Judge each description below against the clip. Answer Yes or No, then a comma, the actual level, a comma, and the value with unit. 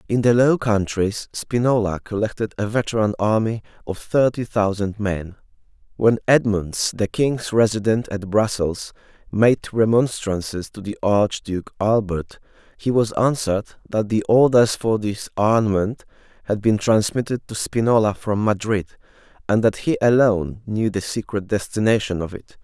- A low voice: Yes, low, 105 Hz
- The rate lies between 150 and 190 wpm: No, average, 140 wpm